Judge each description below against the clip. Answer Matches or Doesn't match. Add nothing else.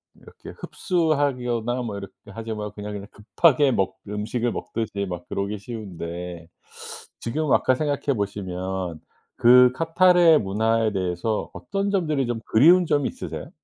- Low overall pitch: Matches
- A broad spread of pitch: Matches